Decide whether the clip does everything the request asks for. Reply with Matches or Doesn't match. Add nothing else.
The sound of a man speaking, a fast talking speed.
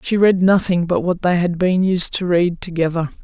Doesn't match